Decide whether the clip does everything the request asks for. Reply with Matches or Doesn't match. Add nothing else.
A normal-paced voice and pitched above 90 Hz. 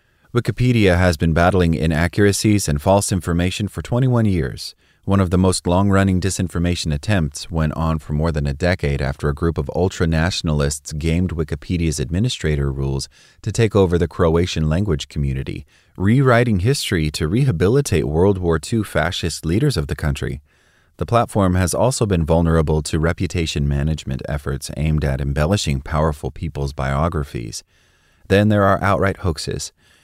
Doesn't match